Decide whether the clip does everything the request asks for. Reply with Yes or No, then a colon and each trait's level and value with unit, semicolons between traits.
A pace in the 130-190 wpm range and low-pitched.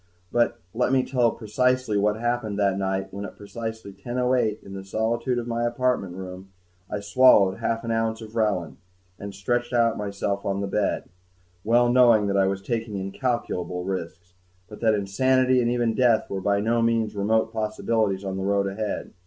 Yes: average, 180 wpm; low, 110 Hz